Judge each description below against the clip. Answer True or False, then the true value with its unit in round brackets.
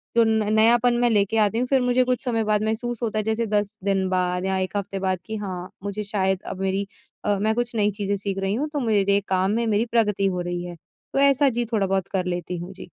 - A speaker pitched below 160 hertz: False (205 Hz)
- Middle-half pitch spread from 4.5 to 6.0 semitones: False (3.0 semitones)